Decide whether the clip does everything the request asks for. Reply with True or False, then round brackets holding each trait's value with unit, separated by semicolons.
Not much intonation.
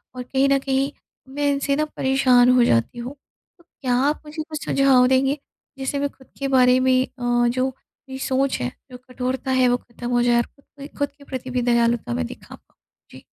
True (1.9 semitones)